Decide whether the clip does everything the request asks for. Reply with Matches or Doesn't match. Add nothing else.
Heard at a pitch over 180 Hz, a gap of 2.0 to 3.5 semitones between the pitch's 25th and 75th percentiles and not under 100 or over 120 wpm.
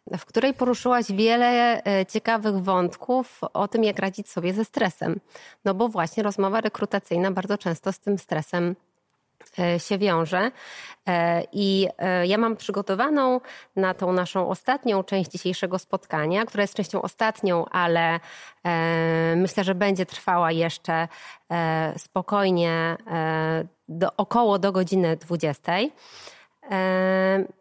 Matches